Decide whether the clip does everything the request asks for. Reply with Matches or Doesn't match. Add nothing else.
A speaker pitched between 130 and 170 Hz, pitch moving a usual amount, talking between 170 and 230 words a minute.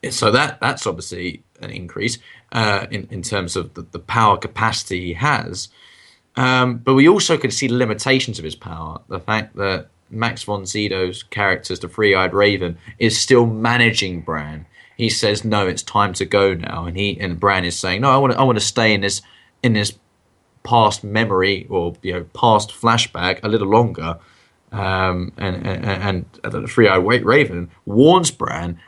Doesn't match